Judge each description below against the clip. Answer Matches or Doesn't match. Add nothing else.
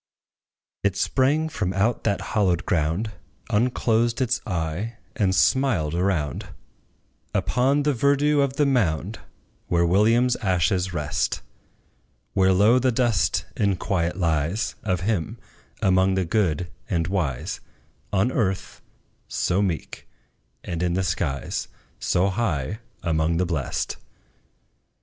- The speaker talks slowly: Matches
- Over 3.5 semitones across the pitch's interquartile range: Matches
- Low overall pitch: Matches